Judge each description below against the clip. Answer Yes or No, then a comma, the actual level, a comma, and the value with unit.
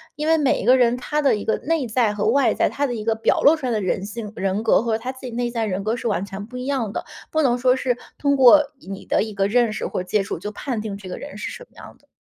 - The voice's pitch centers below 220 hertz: No, high, 235 Hz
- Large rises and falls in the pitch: No, average, 3.9 semitones